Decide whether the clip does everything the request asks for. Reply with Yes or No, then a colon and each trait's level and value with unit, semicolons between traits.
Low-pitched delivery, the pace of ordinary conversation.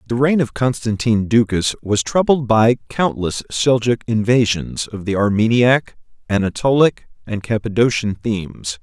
No: low, 115 Hz; slow, 120 wpm